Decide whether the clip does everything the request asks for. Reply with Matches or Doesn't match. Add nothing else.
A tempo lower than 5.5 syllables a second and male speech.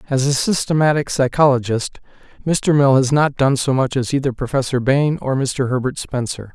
Matches